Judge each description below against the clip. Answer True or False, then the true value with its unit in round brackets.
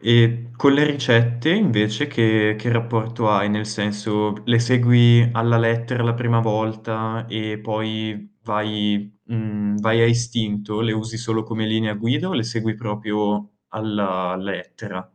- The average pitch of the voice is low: True (110 Hz)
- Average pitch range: False (1.8 semitones)